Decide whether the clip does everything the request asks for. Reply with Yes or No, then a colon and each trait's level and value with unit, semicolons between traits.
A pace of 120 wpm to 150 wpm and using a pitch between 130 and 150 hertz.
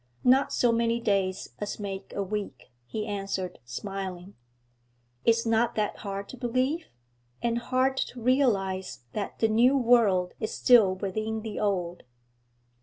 No: average, 140 wpm; high, 215 Hz